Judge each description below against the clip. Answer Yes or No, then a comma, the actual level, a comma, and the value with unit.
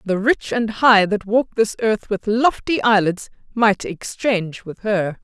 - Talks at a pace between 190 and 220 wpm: No, average, 170 wpm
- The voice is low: No, high, 210 Hz